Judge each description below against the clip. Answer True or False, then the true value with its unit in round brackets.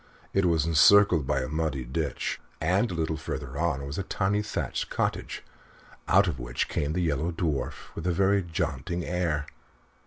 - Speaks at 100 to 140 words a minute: False (175 wpm)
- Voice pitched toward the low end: True (80 Hz)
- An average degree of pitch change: True (4.0 semitones)